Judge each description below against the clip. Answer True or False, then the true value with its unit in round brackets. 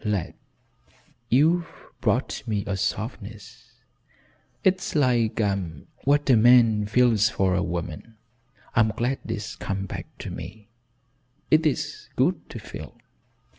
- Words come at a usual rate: False (120 wpm)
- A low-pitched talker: True (110 Hz)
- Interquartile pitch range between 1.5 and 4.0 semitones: True (3.6 semitones)